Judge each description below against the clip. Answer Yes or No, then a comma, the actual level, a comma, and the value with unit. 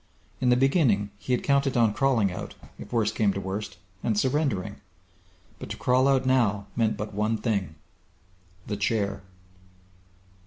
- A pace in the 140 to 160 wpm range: Yes, average, 155 wpm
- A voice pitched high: No, low, 110 Hz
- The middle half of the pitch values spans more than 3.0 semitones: Yes, average, 4.0 semitones